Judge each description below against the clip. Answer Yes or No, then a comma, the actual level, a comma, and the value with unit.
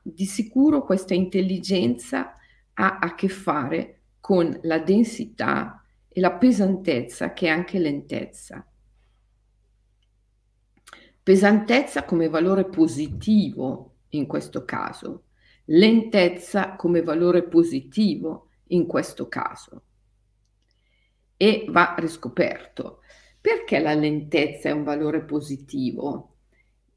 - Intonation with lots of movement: Yes, wide, 6.1 semitones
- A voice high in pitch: No, medium, 170 Hz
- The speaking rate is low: Yes, slow, 95 wpm